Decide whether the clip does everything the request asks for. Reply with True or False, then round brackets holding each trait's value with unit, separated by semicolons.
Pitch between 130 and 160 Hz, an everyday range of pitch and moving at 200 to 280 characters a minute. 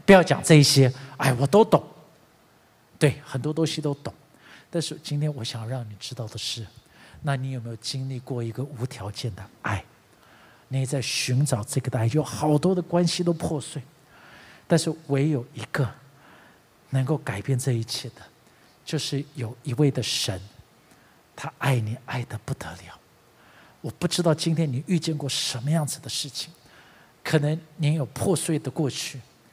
True (140 Hz; 3.7 semitones; 235 characters per minute)